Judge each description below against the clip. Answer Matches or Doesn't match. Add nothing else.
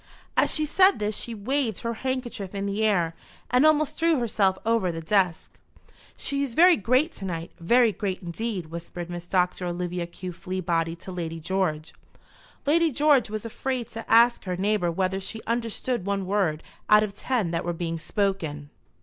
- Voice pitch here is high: Matches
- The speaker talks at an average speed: Matches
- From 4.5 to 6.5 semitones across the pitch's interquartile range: Matches